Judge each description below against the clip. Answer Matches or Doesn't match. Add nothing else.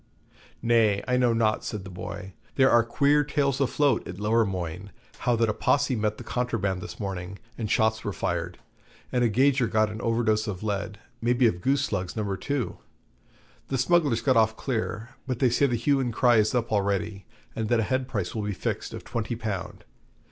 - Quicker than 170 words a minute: Matches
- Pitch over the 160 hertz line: Doesn't match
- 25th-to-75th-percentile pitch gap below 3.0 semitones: Doesn't match